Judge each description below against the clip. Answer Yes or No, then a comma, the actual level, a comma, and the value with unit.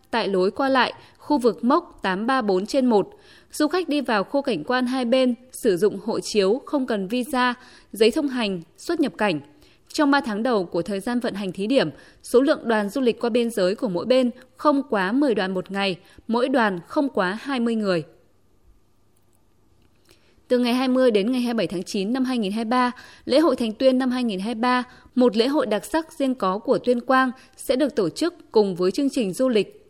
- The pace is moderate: Yes, average, 200 wpm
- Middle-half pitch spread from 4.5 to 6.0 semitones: Yes, average, 4.8 semitones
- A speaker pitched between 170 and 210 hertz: No, high, 240 Hz